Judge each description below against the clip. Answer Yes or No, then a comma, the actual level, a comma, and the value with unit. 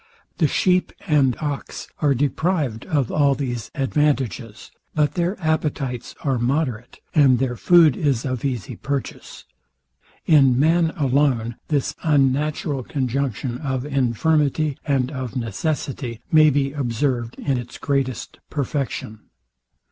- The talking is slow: Yes, slow, 120 wpm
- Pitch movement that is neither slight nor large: Yes, average, 3.2 semitones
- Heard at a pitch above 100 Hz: Yes, medium, 140 Hz